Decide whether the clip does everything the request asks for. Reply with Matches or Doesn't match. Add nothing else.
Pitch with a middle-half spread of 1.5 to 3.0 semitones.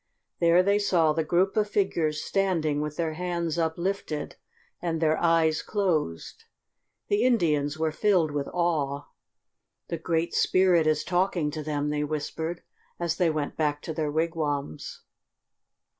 Matches